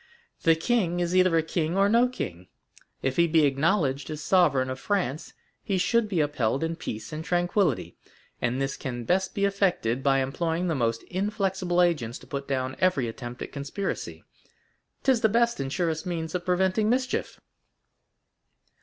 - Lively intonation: Yes, wide, 5.7 semitones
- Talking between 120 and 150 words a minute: No, average, 165 wpm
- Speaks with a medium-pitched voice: Yes, medium, 165 Hz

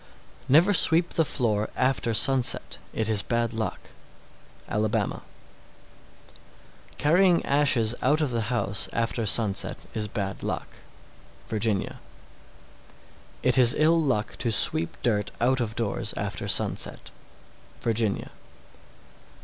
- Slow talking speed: Yes, slow, 120 wpm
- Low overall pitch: Yes, low, 115 Hz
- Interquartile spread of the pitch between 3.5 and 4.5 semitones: Yes, average, 3.9 semitones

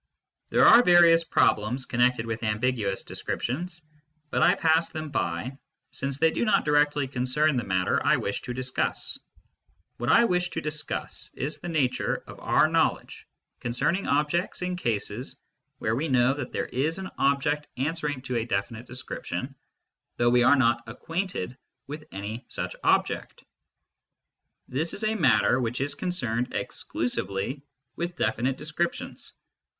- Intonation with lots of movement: No, average, 4.9 semitones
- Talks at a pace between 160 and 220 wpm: No, slow, 135 wpm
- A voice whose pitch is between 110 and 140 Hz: Yes, low, 135 Hz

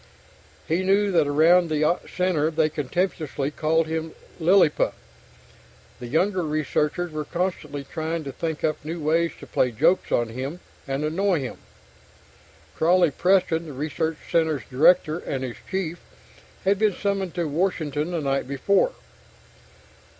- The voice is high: No, medium, 160 Hz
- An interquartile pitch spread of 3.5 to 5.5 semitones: No, average, 3.1 semitones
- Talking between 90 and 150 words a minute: Yes, average, 140 wpm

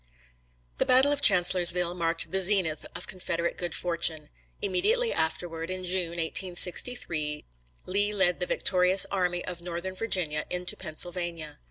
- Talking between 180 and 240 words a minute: No, slow, 135 wpm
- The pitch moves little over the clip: Yes, narrow, 2.0 semitones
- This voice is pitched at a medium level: Yes, medium, 180 Hz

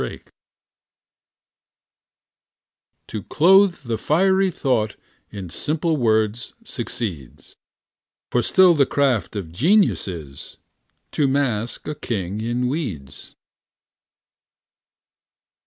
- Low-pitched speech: Yes, low, 120 Hz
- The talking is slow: Yes, slow, 90 wpm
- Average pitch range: No, wide, 6.8 semitones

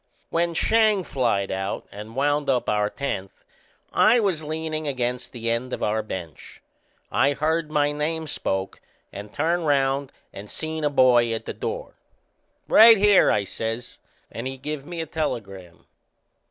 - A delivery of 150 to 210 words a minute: Yes, average, 160 wpm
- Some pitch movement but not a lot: No, wide, 5.9 semitones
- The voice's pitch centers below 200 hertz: Yes, medium, 140 Hz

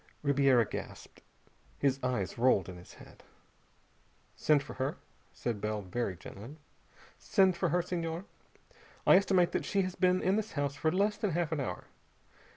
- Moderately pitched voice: Yes, medium, 145 Hz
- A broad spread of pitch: Yes, wide, 6.9 semitones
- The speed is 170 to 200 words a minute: No, average, 160 wpm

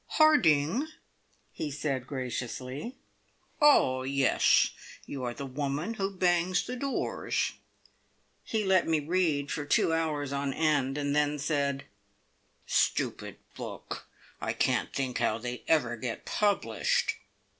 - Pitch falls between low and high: Yes, medium, 145 Hz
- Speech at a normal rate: No, slow, 125 wpm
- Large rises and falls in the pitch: No, average, 4.7 semitones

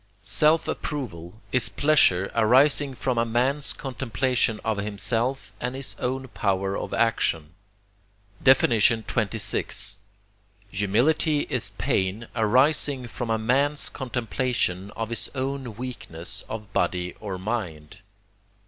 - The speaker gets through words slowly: Yes, slow, 110 wpm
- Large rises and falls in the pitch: No, average, 4.5 semitones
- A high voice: No, low, 115 Hz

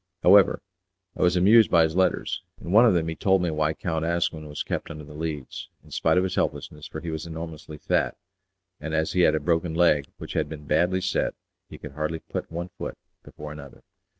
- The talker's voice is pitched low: Yes, very low, 80 Hz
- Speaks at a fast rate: Yes, fast, 220 wpm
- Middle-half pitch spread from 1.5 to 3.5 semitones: Yes, narrow, 2.5 semitones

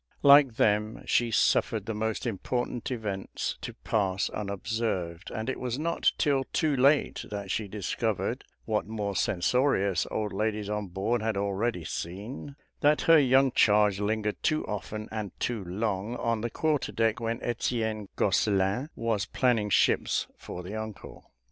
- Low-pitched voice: Yes, low, 110 Hz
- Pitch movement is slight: No, average, 3.2 semitones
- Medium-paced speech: Yes, average, 150 wpm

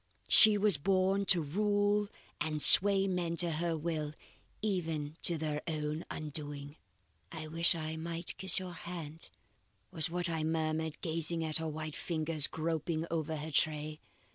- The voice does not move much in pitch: Yes, narrow, 2.2 semitones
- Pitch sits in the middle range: Yes, medium, 160 Hz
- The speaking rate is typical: Yes, average, 150 wpm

